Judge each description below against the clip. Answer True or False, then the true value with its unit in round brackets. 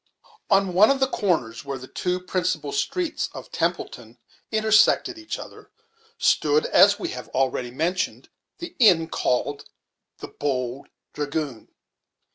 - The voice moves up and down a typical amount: False (7.8 semitones)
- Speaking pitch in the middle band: True (180 Hz)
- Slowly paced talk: True (130 wpm)